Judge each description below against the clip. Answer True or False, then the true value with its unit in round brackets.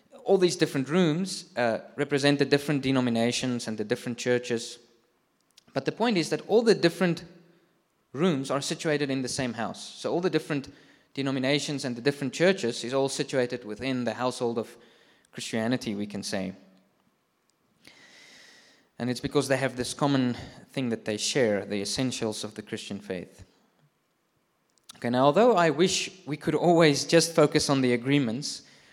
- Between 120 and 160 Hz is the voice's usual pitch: True (135 Hz)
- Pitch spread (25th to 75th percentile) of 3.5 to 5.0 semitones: True (4.4 semitones)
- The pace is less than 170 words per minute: True (160 wpm)